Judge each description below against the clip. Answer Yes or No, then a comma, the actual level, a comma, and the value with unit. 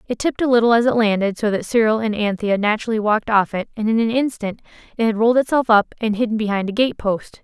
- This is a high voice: Yes, high, 220 Hz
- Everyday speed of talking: No, fast, 250 wpm